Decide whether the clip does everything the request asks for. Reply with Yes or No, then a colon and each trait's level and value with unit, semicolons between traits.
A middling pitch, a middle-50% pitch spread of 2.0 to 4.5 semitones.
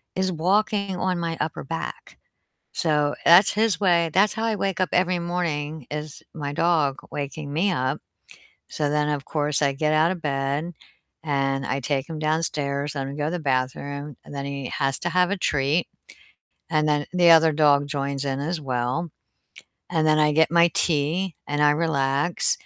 Yes: medium, 150 Hz; average, 3.4 semitones